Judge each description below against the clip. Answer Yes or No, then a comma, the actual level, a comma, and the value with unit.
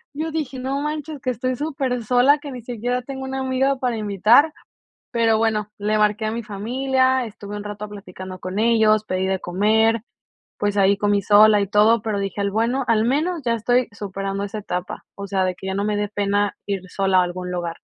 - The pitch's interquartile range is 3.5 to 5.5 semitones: Yes, average, 4.0 semitones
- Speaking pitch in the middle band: No, high, 215 Hz